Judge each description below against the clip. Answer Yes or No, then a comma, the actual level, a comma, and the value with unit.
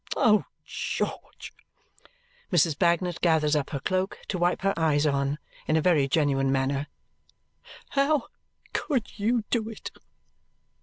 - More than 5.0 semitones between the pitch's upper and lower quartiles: Yes, wide, 5.5 semitones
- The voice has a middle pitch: Yes, medium, 165 Hz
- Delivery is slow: Yes, slow, 130 wpm